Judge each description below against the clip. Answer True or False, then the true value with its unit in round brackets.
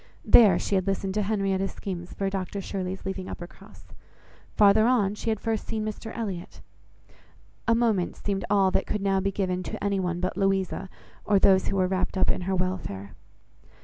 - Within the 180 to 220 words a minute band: True (185 wpm)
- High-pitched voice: True (195 Hz)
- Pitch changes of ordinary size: False (1.7 semitones)